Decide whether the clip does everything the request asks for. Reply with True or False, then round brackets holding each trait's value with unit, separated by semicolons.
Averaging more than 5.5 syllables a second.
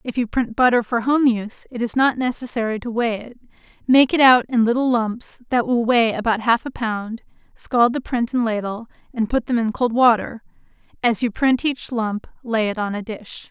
False (5.0 syllables/s)